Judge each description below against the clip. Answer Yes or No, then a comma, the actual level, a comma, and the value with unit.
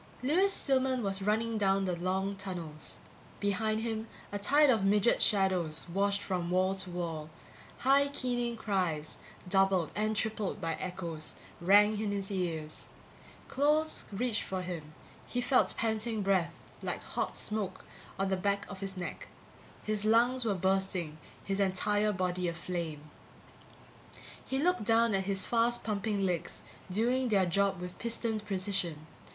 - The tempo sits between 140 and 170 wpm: Yes, average, 145 wpm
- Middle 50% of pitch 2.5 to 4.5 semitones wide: Yes, average, 3.4 semitones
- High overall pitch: Yes, high, 195 Hz